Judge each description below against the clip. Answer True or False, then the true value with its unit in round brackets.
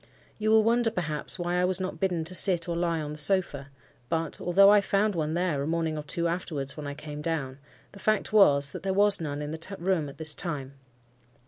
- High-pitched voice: False (170 Hz)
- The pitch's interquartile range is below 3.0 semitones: False (4.1 semitones)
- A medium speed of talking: False (230 wpm)